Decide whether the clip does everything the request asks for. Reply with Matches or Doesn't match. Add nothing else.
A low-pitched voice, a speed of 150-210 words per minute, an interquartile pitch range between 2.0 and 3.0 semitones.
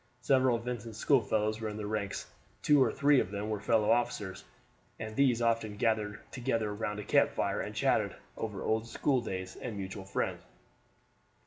Matches